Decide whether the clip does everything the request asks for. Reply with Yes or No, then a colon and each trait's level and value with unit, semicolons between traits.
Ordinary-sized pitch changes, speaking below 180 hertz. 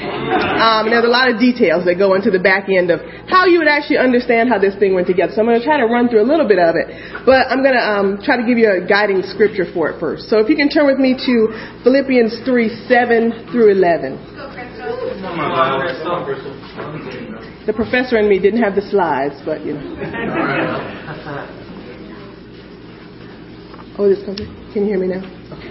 No: average, 3.8 semitones; high, 220 Hz